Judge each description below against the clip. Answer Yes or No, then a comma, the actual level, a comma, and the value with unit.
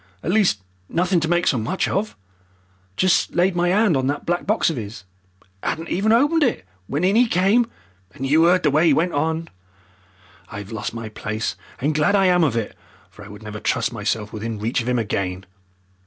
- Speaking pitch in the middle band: Yes, medium, 155 Hz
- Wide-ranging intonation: Yes, wide, 8.4 semitones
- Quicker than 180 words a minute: Yes, fast, 205 wpm